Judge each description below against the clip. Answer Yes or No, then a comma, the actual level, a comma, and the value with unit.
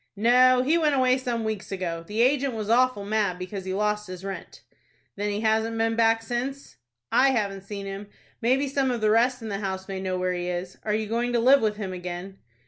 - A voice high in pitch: Yes, high, 215 Hz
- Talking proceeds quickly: Yes, fast, 225 wpm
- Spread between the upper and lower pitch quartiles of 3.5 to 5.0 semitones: Yes, average, 3.9 semitones